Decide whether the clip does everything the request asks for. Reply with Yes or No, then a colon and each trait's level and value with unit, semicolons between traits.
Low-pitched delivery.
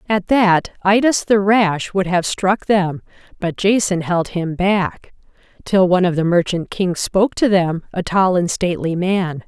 No: medium, 185 Hz